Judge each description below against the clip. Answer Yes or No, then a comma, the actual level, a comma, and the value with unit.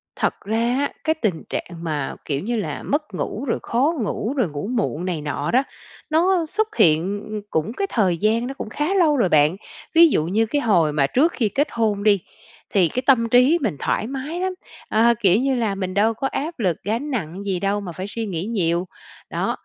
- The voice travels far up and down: Yes, wide, 6.7 semitones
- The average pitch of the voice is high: Yes, high, 220 Hz